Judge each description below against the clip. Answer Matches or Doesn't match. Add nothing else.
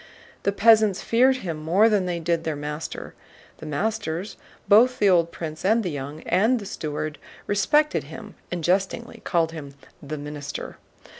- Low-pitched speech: Doesn't match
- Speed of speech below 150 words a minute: Doesn't match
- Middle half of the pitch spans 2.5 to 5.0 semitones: Doesn't match